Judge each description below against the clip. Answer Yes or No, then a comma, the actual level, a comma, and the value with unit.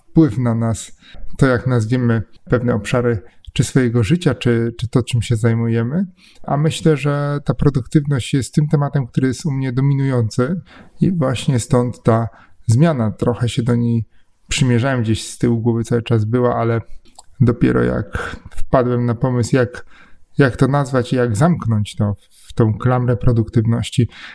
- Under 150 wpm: No, fast, 160 wpm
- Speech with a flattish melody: No, average, 3.2 semitones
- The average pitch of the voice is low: Yes, low, 120 Hz